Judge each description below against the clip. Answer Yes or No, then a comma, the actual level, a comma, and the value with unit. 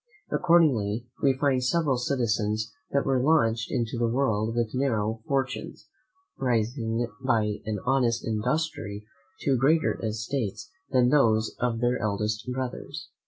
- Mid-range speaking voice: No, low, 120 Hz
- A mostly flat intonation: No, average, 3.4 semitones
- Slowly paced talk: Yes, slow, 125 wpm